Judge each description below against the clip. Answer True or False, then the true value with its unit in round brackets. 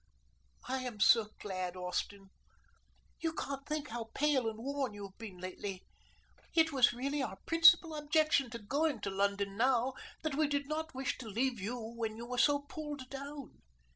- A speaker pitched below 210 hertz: False (255 Hz)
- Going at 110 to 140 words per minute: False (175 wpm)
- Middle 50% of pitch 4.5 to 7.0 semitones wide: True (5.4 semitones)